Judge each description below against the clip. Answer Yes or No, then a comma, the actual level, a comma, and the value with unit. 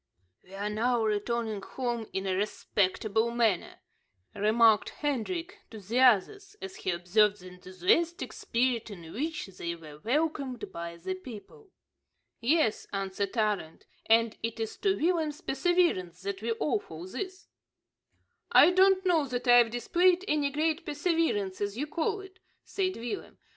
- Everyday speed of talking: Yes, average, 145 wpm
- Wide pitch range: Yes, wide, 8.3 semitones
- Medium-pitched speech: No, high, 235 Hz